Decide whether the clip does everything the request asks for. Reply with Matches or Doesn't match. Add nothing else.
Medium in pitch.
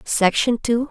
Doesn't match